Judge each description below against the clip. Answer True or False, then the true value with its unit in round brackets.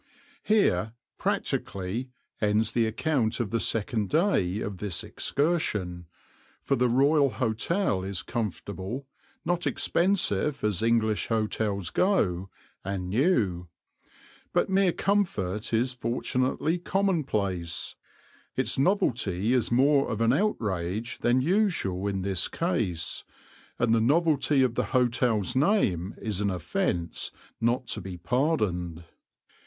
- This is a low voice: True (115 Hz)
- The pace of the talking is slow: True (120 wpm)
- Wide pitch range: True (6.4 semitones)